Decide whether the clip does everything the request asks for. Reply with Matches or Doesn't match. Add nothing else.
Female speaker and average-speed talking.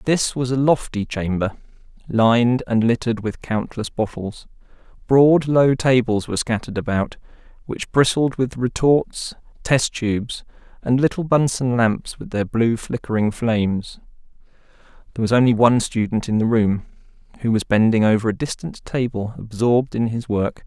Doesn't match